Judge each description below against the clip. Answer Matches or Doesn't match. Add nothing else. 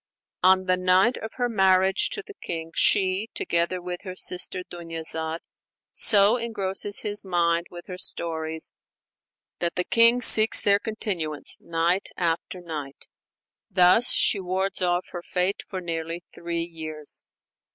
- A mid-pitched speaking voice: Matches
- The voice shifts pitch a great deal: Doesn't match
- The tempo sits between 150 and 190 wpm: Doesn't match